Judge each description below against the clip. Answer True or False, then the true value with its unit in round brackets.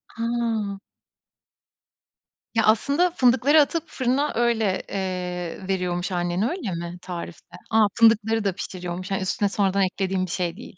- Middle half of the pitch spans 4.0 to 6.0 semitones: True (4.3 semitones)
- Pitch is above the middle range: True (200 Hz)